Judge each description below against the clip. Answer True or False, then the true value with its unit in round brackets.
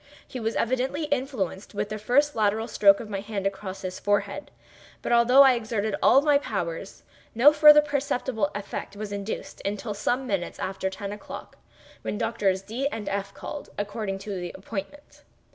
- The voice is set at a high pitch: True (215 Hz)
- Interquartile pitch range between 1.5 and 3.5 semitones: False (4.7 semitones)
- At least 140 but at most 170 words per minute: True (165 wpm)